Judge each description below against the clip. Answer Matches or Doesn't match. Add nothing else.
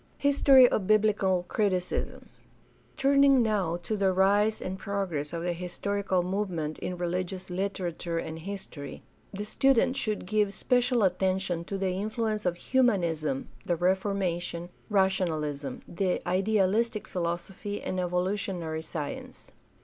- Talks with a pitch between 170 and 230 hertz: Matches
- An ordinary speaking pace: Doesn't match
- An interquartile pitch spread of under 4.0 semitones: Matches